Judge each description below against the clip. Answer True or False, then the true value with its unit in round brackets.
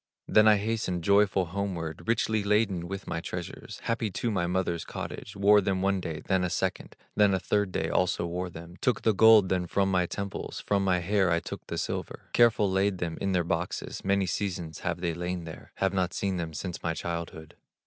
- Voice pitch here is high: False (95 Hz)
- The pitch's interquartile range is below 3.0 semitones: True (2.6 semitones)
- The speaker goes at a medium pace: False (210 wpm)